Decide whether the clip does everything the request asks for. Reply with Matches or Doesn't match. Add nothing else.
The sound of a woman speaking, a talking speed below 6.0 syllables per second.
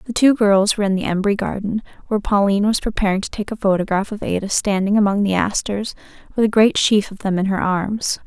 Doesn't match